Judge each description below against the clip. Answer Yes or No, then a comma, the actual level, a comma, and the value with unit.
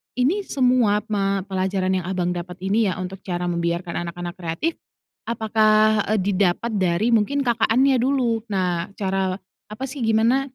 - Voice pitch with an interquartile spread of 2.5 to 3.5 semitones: No, average, 4.1 semitones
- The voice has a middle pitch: No, high, 200 Hz